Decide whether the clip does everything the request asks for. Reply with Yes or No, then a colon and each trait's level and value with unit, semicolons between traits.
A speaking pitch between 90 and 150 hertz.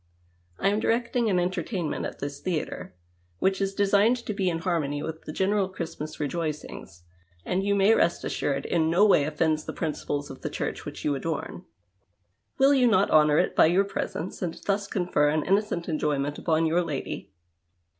No: medium, 170 Hz